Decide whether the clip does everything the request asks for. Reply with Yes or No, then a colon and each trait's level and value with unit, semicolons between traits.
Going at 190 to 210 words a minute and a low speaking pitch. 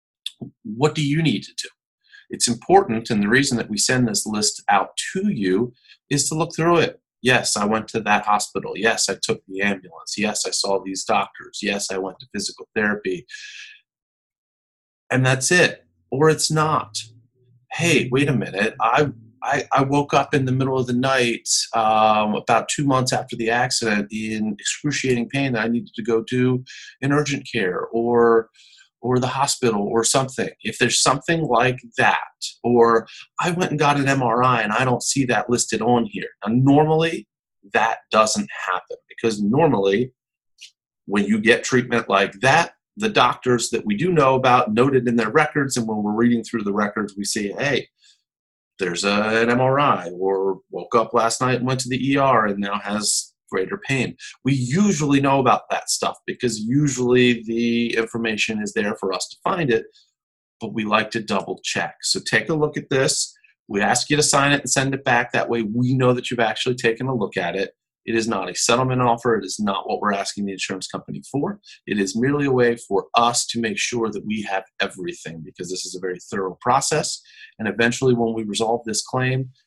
Yes: average, 195 wpm; low, 120 Hz